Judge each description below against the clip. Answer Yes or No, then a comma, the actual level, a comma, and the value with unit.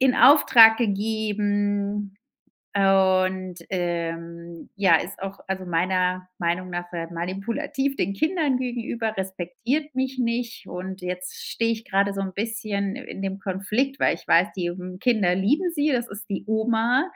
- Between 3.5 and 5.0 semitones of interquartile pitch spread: Yes, average, 4.2 semitones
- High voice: Yes, high, 200 Hz